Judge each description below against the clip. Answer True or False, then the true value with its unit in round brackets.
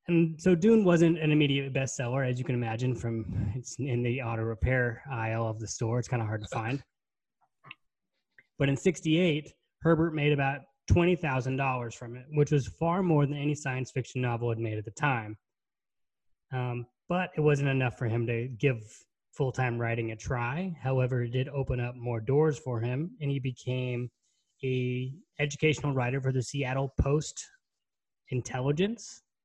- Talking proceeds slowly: False (170 wpm)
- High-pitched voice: False (130 Hz)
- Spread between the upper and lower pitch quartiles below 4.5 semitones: True (3.4 semitones)